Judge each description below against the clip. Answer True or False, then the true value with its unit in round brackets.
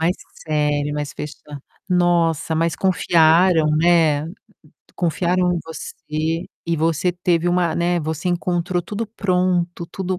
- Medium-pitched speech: True (170 Hz)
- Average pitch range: False (2.0 semitones)